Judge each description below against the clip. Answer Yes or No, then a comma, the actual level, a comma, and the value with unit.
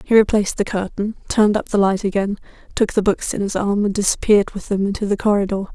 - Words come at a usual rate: No, fast, 230 wpm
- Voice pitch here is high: Yes, high, 200 Hz